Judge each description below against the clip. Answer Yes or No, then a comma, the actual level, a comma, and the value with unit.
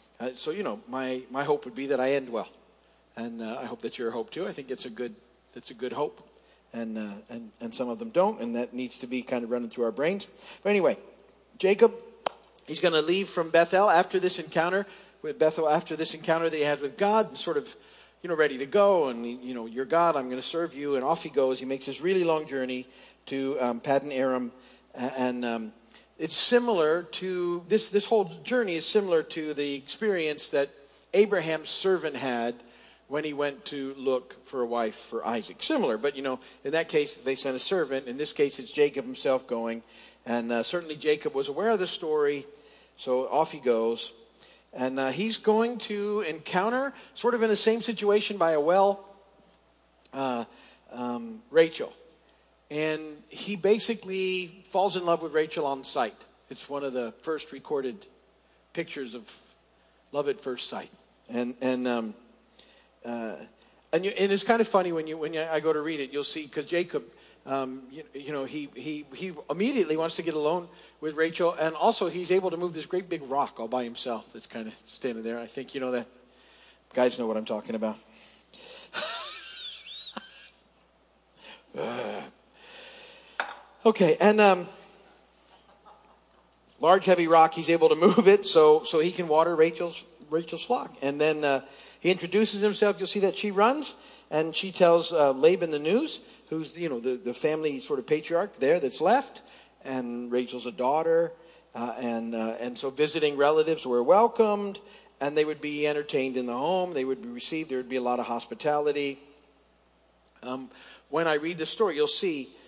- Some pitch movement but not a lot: No, wide, 6.2 semitones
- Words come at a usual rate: Yes, average, 190 wpm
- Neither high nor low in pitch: Yes, medium, 150 Hz